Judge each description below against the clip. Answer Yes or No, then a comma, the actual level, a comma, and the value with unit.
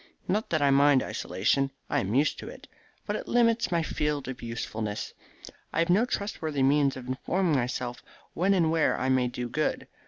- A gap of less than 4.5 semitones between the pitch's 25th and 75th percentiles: No, average, 4.9 semitones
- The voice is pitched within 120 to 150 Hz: Yes, medium, 140 Hz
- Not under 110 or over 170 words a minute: No, average, 190 wpm